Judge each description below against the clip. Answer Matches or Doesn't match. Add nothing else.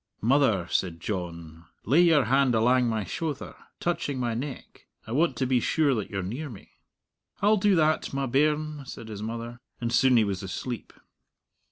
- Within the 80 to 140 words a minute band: Doesn't match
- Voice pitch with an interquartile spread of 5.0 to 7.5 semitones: Matches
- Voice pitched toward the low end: Matches